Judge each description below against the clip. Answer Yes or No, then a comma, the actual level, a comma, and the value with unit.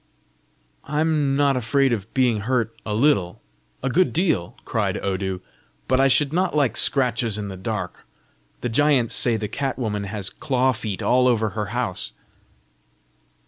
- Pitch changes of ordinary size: Yes, average, 4.6 semitones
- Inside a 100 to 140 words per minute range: No, average, 155 wpm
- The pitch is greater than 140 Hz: No, low, 120 Hz